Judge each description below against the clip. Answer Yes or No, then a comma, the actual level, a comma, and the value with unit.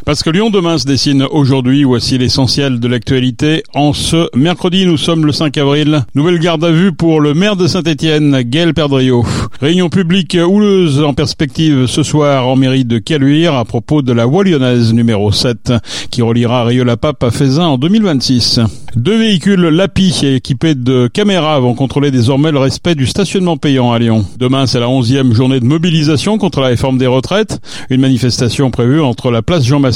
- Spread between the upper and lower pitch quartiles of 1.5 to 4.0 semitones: No, average, 4.5 semitones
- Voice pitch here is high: No, medium, 140 Hz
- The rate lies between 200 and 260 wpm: No, average, 185 wpm